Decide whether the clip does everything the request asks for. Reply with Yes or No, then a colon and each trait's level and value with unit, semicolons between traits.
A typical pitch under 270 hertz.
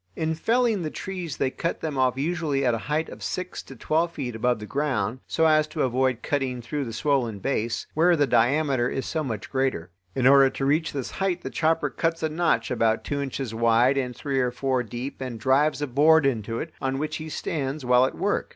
Yes: low, 135 Hz